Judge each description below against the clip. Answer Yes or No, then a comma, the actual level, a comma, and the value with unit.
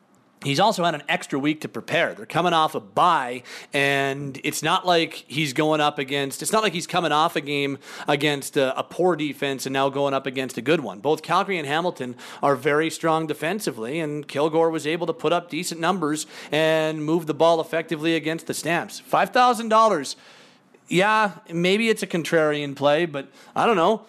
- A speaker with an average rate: Yes, average, 195 wpm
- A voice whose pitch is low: No, medium, 160 Hz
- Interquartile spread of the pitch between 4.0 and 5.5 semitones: No, average, 3.3 semitones